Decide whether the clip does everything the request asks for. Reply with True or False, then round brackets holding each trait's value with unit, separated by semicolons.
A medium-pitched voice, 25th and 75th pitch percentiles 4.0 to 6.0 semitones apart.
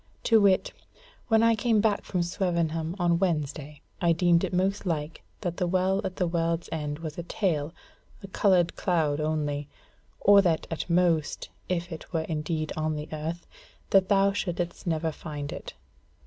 False (170 Hz; 3.1 semitones)